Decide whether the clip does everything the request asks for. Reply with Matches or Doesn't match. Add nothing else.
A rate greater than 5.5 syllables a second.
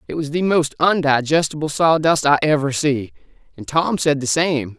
Doesn't match